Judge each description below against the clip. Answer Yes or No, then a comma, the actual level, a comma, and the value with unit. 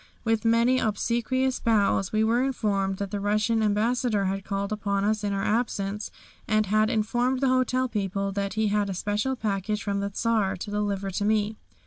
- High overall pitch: Yes, high, 210 Hz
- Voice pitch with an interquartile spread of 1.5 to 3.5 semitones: Yes, narrow, 2.4 semitones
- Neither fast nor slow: Yes, average, 185 wpm